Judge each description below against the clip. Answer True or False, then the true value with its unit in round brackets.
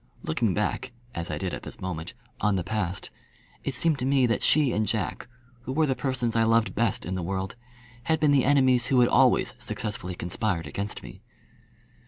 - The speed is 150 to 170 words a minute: False (205 wpm)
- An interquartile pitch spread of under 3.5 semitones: False (5.6 semitones)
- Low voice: True (115 Hz)